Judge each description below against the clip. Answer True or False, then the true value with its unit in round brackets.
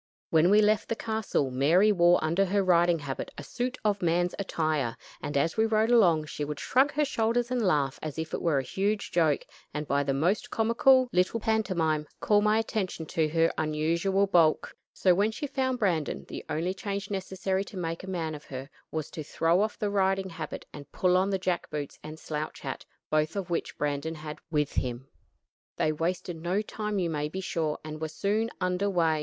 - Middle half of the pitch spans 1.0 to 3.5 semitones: False (4.7 semitones)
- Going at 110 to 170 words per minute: False (205 wpm)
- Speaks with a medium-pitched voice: True (175 Hz)